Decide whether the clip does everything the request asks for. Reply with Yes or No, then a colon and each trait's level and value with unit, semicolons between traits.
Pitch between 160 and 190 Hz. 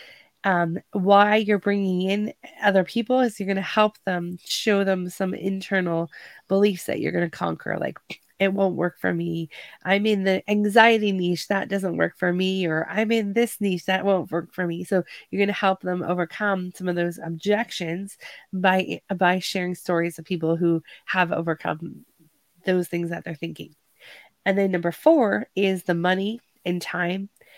Yes: medium, 185 Hz